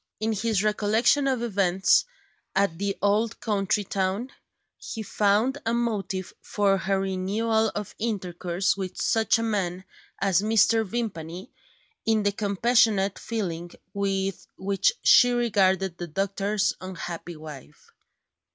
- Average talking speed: No, slow, 125 wpm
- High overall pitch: Yes, high, 200 Hz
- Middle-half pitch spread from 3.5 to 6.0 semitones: No, average, 2.8 semitones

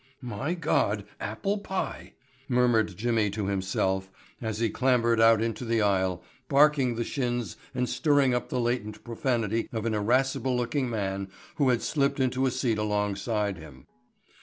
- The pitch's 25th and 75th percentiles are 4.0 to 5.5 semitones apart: No, average, 3.5 semitones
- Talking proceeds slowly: No, average, 155 wpm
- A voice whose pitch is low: Yes, low, 115 Hz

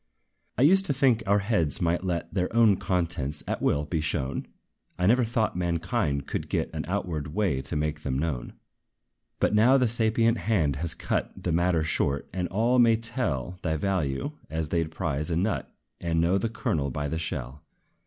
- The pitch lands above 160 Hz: No, very low, 85 Hz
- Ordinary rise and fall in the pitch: No, wide, 6.3 semitones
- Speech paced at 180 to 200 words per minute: Yes, average, 190 wpm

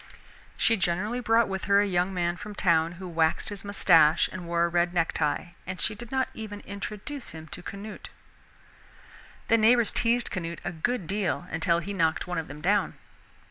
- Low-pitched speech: No, medium, 185 Hz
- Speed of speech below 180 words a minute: No, average, 185 wpm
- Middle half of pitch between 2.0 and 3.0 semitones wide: No, average, 3.7 semitones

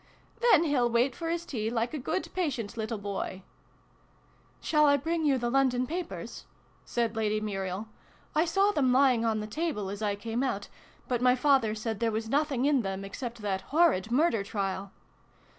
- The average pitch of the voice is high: Yes, high, 240 Hz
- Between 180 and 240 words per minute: Yes, average, 195 wpm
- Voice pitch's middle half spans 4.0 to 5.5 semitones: Yes, average, 5.2 semitones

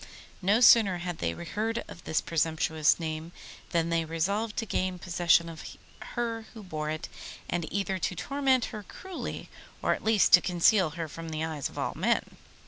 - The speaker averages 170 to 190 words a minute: Yes, average, 180 wpm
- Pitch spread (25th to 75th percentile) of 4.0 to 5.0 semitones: Yes, average, 4.7 semitones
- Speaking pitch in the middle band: Yes, medium, 175 Hz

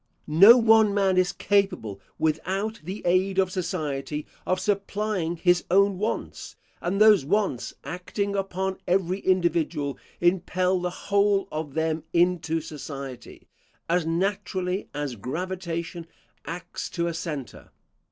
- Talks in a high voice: No, medium, 180 Hz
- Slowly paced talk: Yes, slow, 125 wpm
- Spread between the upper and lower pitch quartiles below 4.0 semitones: Yes, average, 3.2 semitones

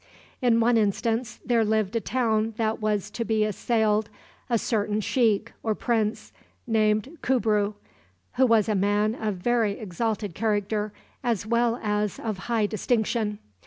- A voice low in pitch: No, high, 220 Hz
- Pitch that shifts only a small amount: Yes, narrow, 1.7 semitones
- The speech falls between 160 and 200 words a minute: No, average, 150 wpm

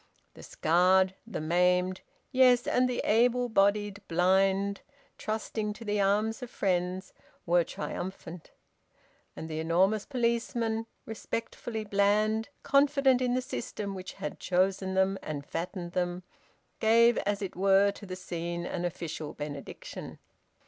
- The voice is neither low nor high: No, high, 195 Hz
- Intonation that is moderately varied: Yes, average, 3.7 semitones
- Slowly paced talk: Yes, slow, 130 wpm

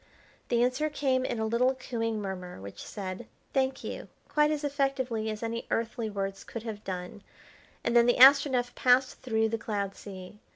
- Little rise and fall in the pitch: No, average, 3.7 semitones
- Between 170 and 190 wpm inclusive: Yes, average, 175 wpm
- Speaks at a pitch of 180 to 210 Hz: No, high, 230 Hz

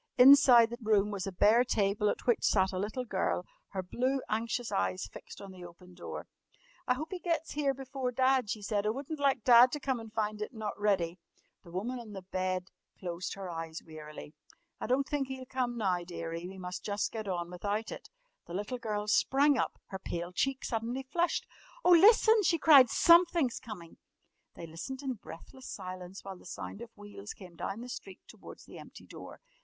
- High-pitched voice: Yes, high, 215 Hz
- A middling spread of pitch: No, wide, 5.8 semitones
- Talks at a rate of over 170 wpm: Yes, average, 200 wpm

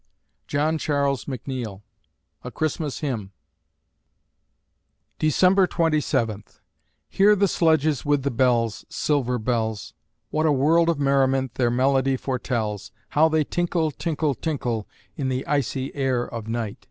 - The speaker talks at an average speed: No, slow, 130 wpm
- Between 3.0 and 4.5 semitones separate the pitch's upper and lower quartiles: Yes, average, 4.2 semitones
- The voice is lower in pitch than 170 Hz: Yes, low, 135 Hz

